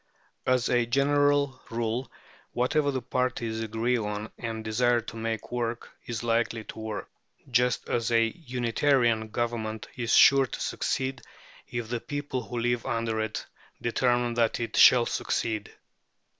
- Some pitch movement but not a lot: No, narrow, 2.0 semitones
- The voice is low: Yes, low, 120 Hz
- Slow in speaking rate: No, average, 145 wpm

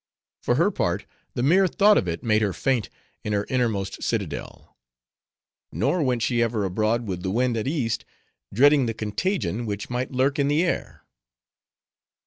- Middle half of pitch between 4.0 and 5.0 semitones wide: Yes, average, 4.5 semitones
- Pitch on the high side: No, low, 120 Hz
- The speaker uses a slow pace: No, average, 165 wpm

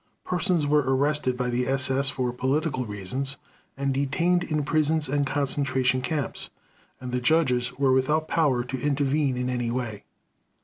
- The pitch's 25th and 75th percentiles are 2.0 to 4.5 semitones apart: Yes, average, 2.8 semitones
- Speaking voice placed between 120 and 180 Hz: Yes, low, 135 Hz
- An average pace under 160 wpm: Yes, average, 150 wpm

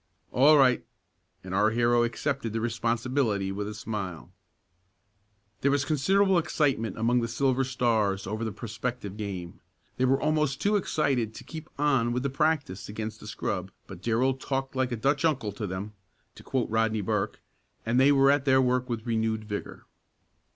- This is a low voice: Yes, low, 120 Hz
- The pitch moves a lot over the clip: No, average, 4.0 semitones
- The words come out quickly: No, average, 170 wpm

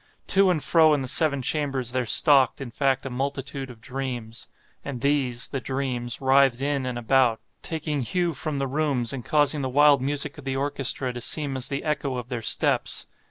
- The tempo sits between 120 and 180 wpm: No, average, 190 wpm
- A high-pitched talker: No, low, 135 Hz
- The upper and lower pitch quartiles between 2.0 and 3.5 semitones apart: Yes, narrow, 2.4 semitones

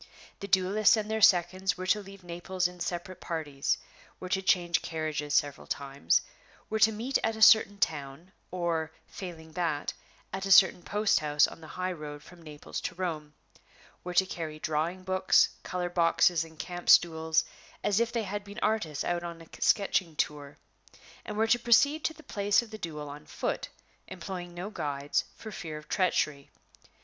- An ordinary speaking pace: Yes, average, 180 wpm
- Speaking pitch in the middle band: Yes, medium, 175 Hz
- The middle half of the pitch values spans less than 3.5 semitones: No, average, 3.9 semitones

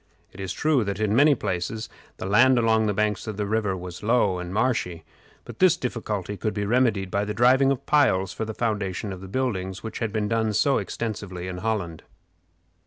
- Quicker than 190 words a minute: Yes, fast, 205 wpm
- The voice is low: Yes, low, 105 Hz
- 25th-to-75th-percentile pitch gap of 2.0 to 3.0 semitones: No, average, 3.4 semitones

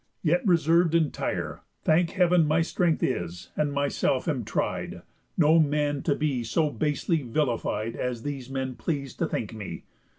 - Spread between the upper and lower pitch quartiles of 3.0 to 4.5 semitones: Yes, average, 3.7 semitones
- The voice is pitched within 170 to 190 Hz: No, medium, 150 Hz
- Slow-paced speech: No, average, 155 wpm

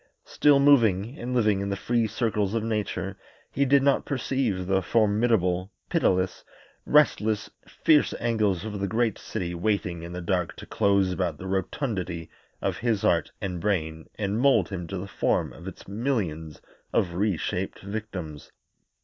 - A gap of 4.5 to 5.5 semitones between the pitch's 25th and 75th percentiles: No, average, 4.0 semitones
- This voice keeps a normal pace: Yes, average, 160 wpm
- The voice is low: Yes, low, 100 Hz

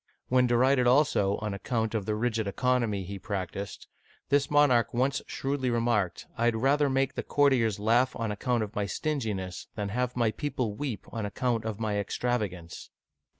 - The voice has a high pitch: No, low, 115 Hz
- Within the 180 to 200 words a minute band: Yes, average, 185 wpm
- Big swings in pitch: No, average, 3.6 semitones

